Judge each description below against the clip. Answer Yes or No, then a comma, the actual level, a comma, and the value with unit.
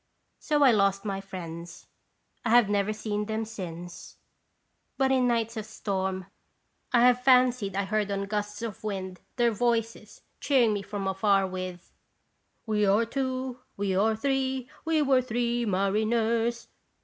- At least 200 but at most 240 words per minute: No, average, 150 wpm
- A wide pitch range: No, average, 3.5 semitones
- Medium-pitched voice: No, high, 215 Hz